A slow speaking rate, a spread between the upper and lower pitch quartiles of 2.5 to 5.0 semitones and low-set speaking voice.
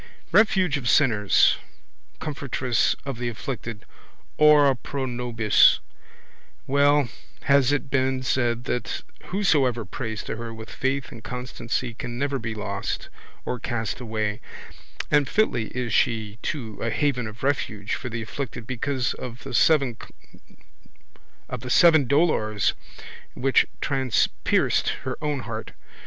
Yes: slow, 120 wpm; average, 3.5 semitones; low, 125 Hz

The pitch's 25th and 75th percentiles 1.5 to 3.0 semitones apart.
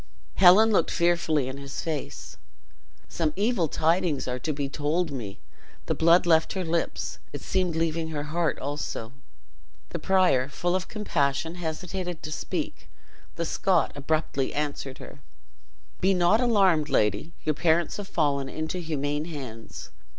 No: average, 3.6 semitones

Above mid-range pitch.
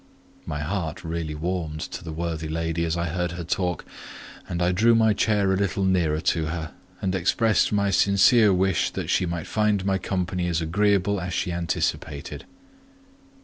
No: very low, 90 Hz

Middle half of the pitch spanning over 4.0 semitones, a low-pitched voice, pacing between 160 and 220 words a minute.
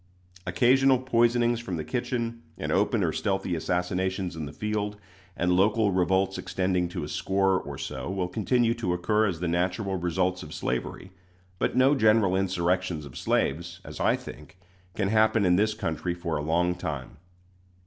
No: average, 3.5 semitones; very low, 95 Hz; average, 170 wpm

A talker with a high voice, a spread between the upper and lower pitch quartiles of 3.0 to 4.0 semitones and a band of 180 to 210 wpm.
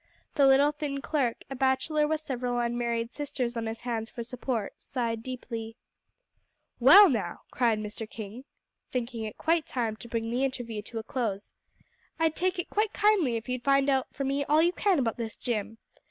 Yes: very high, 250 Hz; average, 3.7 semitones; average, 185 wpm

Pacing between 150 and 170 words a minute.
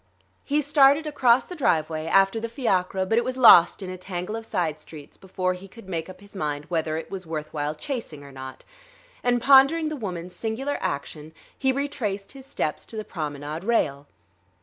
No: average, 195 wpm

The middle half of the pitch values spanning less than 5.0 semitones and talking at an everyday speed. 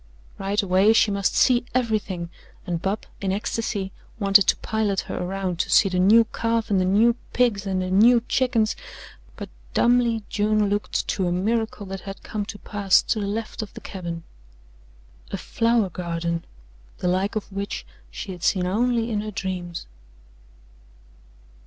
Yes: average, 3.0 semitones; average, 165 wpm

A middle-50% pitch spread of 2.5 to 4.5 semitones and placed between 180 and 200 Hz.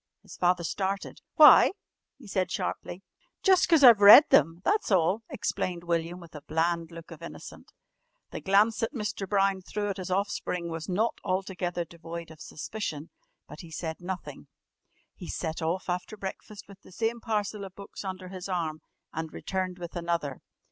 Yes: average, 3.0 semitones; medium, 185 Hz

